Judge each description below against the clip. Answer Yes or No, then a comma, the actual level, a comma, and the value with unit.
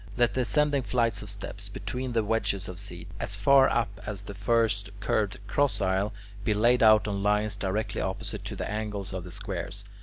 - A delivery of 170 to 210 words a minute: Yes, average, 195 wpm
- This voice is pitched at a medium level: No, low, 105 Hz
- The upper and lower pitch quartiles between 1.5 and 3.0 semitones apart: Yes, narrow, 2.6 semitones